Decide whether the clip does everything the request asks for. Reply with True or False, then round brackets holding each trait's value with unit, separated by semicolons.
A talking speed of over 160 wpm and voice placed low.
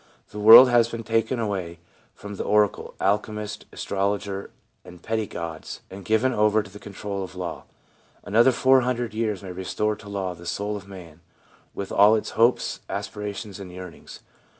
True (170 wpm; 105 Hz)